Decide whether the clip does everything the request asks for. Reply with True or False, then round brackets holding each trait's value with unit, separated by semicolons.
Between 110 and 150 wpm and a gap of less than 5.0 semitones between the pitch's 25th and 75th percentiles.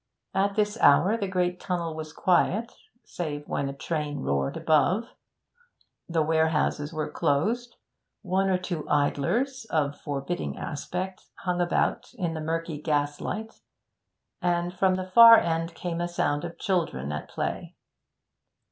True (140 wpm; 3.8 semitones)